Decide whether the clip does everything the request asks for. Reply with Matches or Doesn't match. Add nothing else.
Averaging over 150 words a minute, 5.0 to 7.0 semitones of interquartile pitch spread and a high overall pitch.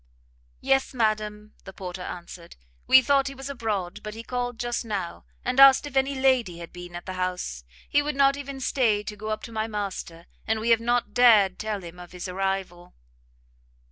Matches